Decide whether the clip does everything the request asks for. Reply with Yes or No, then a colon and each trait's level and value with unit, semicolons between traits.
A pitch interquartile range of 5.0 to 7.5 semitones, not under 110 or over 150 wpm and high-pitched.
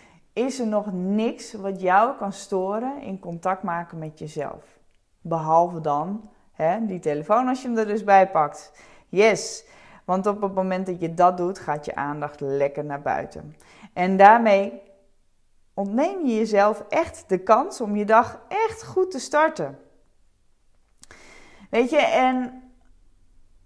Yes: average, 5.3 semitones; average, 145 wpm; high, 195 Hz